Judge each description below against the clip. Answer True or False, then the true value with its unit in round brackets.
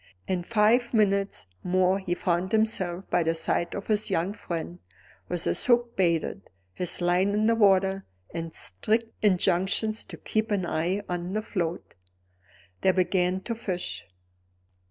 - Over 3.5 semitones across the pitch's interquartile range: False (3.2 semitones)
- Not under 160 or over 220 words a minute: False (150 wpm)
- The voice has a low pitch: False (190 Hz)